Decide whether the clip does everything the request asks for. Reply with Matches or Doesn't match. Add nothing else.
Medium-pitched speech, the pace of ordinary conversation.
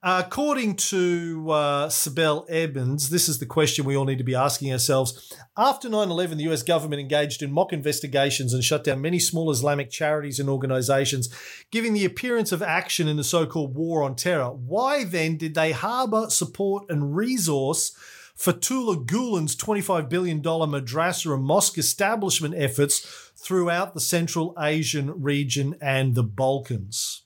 Matches